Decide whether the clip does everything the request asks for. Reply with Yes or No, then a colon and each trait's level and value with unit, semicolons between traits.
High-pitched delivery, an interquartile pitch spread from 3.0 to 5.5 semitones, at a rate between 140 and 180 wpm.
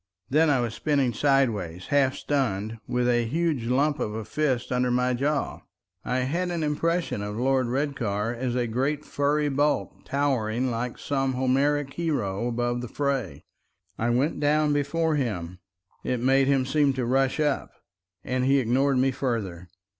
No: low, 130 Hz; average, 3.5 semitones; average, 155 wpm